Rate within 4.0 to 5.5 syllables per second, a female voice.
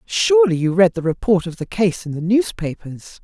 Yes: 5.1 syllables/s; female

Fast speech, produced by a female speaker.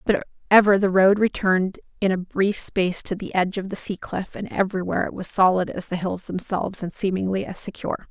Yes: fast, 215 wpm; female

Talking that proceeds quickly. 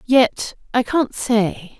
No: slow, 135 wpm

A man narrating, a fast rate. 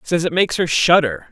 Yes: male; fast, 230 wpm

